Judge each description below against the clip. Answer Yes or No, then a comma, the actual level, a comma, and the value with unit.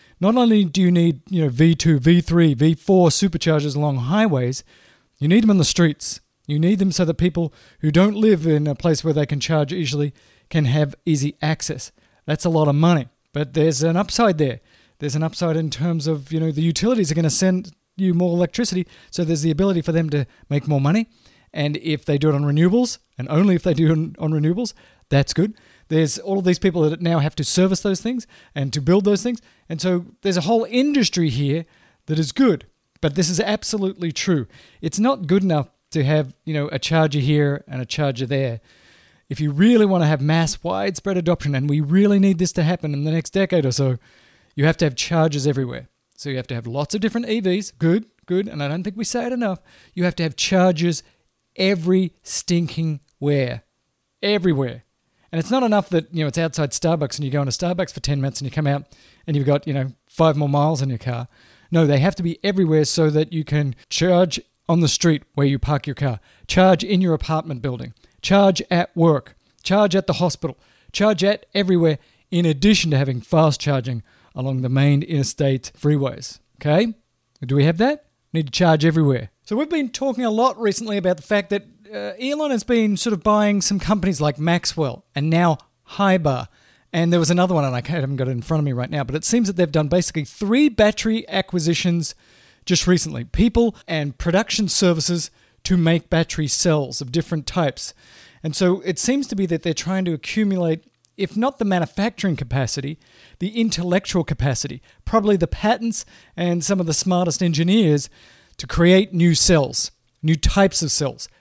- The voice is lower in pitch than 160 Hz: No, medium, 165 Hz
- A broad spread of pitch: No, average, 4.6 semitones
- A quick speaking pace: Yes, fast, 210 wpm